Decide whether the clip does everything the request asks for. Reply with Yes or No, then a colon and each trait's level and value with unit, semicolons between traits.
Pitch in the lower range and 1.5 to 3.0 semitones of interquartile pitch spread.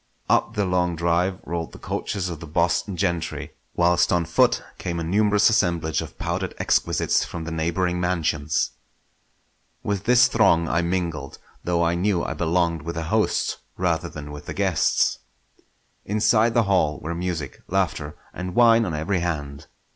Yes: very low, 85 Hz; average, 2.7 semitones